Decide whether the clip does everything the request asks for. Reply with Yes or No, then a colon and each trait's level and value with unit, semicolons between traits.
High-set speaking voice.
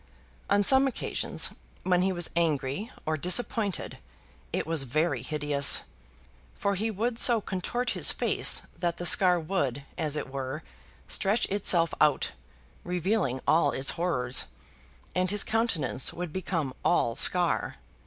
No: medium, 175 Hz